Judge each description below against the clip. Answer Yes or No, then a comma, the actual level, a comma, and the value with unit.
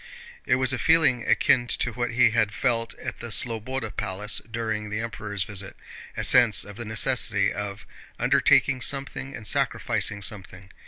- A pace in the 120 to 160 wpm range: Yes, average, 155 wpm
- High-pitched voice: No, low, 115 Hz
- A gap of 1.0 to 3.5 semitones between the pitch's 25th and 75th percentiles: Yes, average, 2.9 semitones